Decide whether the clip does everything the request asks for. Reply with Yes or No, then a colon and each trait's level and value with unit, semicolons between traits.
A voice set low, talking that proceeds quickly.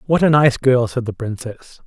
Yes: low, 130 Hz; fast, 225 wpm